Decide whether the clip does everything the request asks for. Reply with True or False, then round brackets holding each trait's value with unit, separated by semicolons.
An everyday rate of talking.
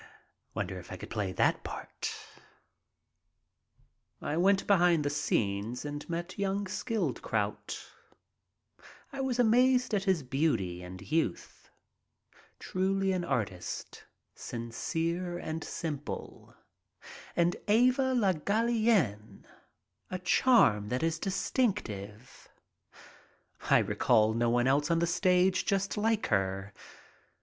False (110 wpm)